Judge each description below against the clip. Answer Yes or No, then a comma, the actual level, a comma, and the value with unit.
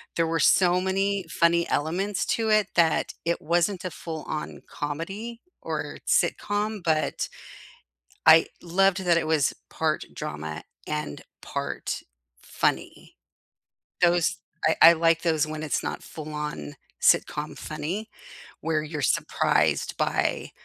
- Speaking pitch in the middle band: Yes, medium, 165 Hz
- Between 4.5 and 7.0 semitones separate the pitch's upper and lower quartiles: No, average, 3.5 semitones